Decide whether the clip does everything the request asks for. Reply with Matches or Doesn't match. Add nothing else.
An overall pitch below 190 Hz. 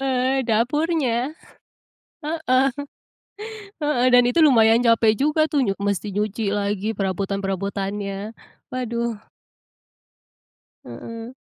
Doesn't match